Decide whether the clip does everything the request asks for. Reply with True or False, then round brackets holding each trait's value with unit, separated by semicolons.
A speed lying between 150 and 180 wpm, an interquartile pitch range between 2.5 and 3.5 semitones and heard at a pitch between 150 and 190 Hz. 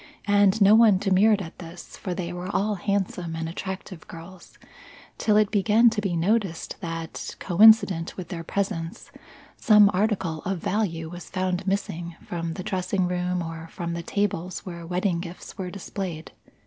True (160 wpm; 3.0 semitones; 185 Hz)